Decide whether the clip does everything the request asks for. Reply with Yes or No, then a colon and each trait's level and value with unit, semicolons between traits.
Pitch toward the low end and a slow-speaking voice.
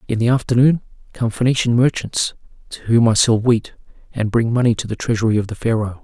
No: low, 115 Hz; average, 200 wpm